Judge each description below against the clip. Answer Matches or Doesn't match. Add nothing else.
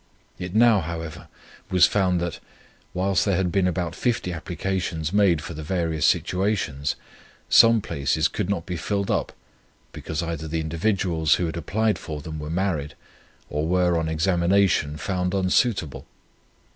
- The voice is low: Matches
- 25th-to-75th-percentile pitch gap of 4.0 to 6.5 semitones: Doesn't match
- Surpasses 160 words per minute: Doesn't match